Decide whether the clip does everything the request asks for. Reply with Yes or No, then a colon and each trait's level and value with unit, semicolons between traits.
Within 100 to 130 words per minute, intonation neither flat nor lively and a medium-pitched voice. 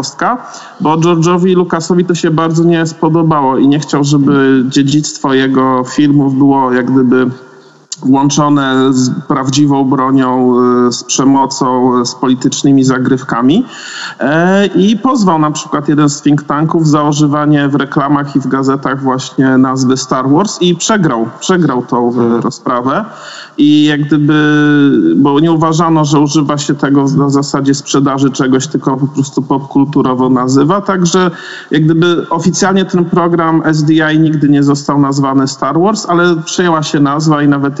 No: average, 140 wpm; average, 3.2 semitones; medium, 145 Hz